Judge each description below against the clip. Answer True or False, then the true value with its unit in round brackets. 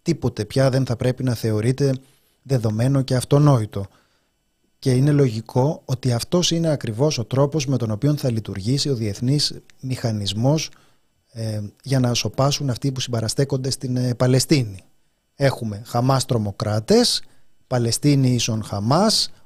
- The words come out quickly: False (135 wpm)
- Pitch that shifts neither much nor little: True (3.4 semitones)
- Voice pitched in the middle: False (130 Hz)